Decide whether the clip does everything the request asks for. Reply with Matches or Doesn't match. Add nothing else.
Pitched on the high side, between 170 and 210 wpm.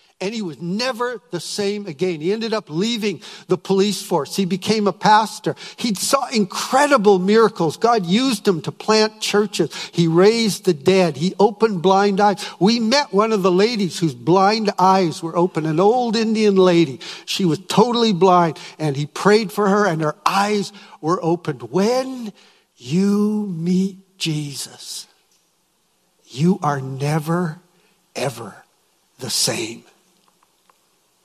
Doesn't match